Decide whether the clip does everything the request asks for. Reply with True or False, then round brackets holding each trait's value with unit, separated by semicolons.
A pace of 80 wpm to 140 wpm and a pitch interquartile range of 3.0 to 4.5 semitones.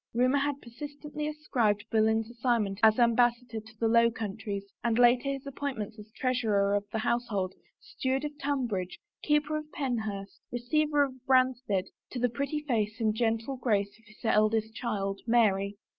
False (165 wpm; 3.5 semitones)